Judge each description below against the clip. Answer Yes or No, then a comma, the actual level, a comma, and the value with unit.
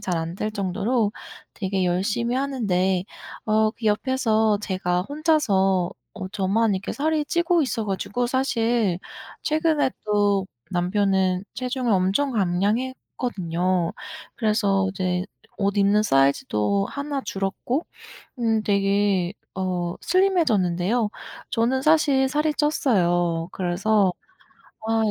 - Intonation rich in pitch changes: No, average, 5.0 semitones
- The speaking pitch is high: Yes, high, 205 Hz